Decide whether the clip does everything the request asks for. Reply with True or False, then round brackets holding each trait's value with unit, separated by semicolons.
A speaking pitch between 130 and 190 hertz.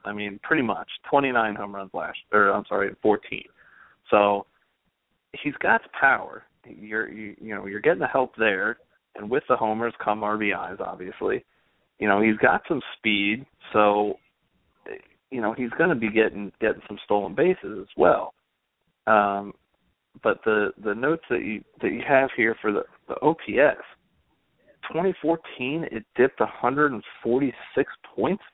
False (110 Hz)